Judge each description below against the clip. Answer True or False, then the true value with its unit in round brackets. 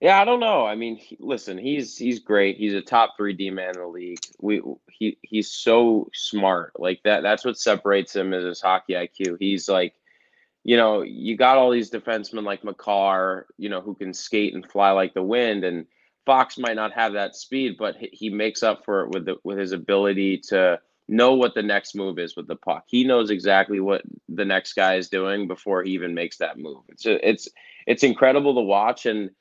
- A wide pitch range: False (3.3 semitones)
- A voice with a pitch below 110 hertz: True (100 Hz)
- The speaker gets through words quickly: True (220 wpm)